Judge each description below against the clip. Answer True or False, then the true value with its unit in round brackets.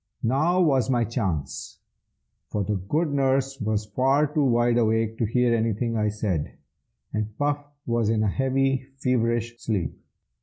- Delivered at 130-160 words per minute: True (150 wpm)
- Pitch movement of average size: True (3.8 semitones)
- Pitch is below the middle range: True (120 Hz)